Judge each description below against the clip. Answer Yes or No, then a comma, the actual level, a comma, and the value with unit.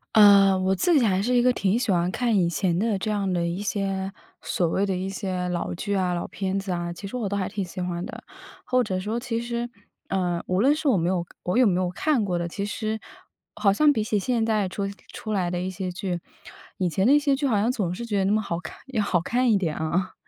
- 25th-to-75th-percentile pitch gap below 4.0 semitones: Yes, average, 3.5 semitones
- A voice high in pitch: Yes, high, 195 Hz